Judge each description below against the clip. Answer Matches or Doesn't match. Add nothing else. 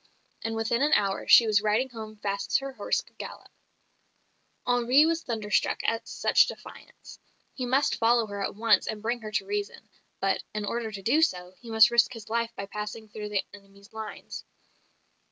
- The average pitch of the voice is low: Doesn't match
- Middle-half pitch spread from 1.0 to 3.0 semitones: Matches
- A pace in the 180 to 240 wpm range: Matches